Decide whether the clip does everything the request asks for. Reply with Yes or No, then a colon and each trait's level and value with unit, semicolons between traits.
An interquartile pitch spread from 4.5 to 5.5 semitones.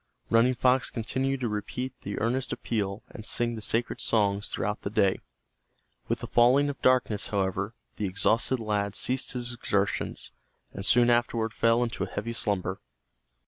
No: average, 3.1 semitones